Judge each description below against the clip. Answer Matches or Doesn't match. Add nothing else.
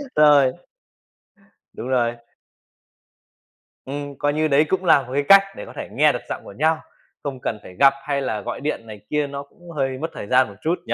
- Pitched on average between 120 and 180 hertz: Matches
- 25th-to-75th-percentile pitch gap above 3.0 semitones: Doesn't match